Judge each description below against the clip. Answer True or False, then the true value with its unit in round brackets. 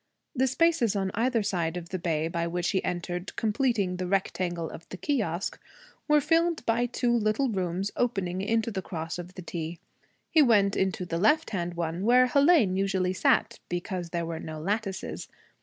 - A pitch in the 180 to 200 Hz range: True (190 Hz)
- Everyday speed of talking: True (180 wpm)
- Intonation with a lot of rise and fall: False (4.9 semitones)